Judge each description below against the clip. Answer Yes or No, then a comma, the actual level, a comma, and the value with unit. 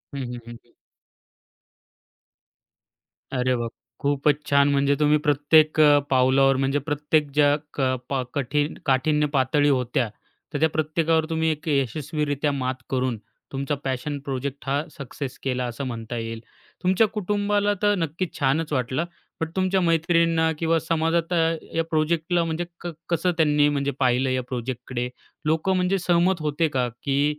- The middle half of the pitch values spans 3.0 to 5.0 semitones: Yes, average, 3.4 semitones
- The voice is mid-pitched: Yes, medium, 145 Hz